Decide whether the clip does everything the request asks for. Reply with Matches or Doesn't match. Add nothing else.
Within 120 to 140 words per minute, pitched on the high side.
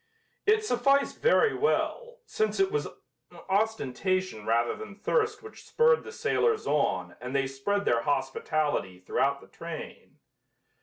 Matches